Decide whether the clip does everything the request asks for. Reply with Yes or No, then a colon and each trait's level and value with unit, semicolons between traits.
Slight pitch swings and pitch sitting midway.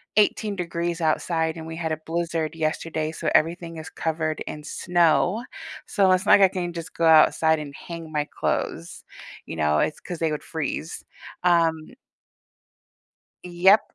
Yes: narrow, 1.7 semitones; medium, 165 Hz